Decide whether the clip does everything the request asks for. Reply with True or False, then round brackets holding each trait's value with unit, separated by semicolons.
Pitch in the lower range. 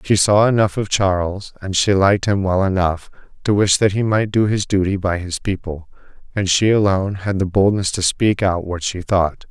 True (95 Hz)